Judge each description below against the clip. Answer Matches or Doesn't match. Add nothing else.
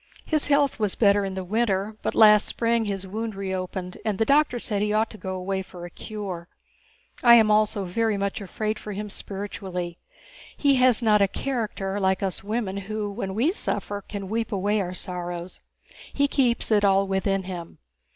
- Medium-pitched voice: Doesn't match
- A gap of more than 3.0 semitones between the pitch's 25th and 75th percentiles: Doesn't match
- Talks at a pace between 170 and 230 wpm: Matches